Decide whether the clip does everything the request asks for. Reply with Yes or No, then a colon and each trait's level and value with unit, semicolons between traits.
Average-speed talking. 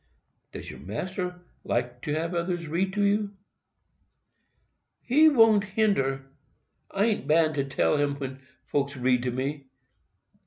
No: slow, 125 wpm